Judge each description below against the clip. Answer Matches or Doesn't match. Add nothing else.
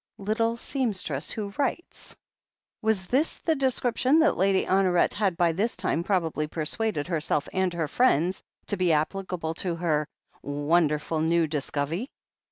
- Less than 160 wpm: Matches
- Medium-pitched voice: Matches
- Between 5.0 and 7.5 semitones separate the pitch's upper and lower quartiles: Matches